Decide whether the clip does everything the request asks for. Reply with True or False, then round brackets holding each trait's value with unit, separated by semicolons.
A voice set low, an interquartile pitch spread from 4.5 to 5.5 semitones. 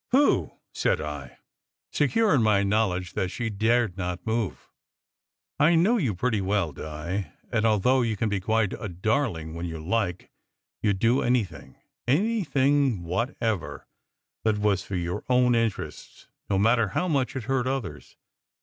True (110 Hz; 5.2 semitones)